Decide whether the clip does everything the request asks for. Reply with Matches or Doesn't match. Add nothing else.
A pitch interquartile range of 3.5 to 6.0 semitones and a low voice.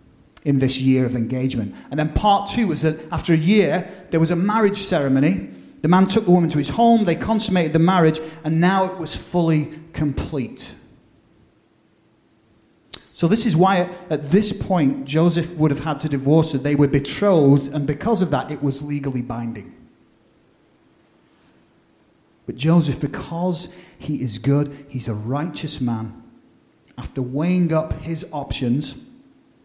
Doesn't match